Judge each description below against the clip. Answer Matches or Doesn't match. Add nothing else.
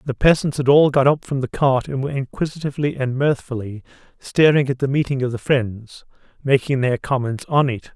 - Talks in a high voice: Doesn't match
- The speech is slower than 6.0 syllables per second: Matches